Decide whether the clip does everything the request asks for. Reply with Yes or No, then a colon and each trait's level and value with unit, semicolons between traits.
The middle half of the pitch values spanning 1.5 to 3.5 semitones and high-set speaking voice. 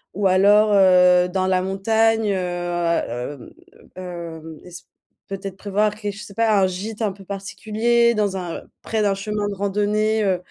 Yes: narrow, 2.4 semitones; high, 200 Hz